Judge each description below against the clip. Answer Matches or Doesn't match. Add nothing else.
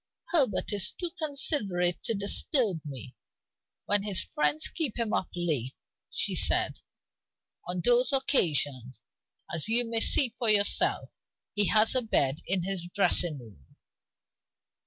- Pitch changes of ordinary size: Doesn't match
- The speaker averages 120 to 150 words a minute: Matches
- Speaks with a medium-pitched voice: Doesn't match